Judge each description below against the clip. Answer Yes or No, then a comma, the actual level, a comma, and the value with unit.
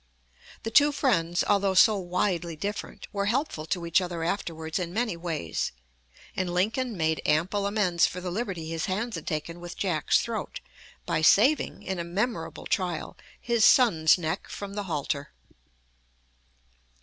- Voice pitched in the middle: Yes, medium, 180 Hz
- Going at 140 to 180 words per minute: Yes, average, 150 wpm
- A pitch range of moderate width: Yes, average, 3.9 semitones